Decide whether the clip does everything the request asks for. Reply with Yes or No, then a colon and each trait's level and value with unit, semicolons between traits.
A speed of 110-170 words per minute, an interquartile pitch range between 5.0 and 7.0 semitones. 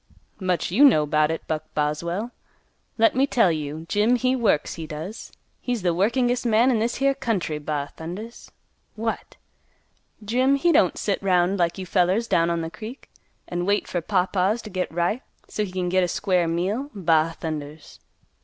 No: average, 180 wpm; wide, 5.4 semitones